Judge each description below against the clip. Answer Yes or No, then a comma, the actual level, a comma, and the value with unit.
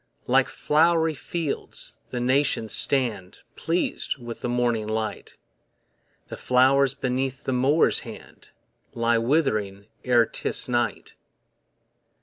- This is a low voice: Yes, low, 125 Hz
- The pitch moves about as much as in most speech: Yes, average, 3.0 semitones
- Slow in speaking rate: Yes, slow, 110 wpm